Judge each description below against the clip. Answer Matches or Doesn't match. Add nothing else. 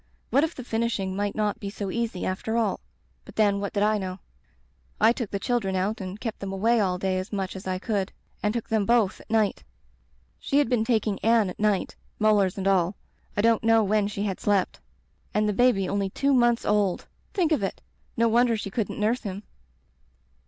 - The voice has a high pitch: Matches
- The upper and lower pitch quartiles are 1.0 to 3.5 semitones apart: Matches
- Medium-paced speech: Doesn't match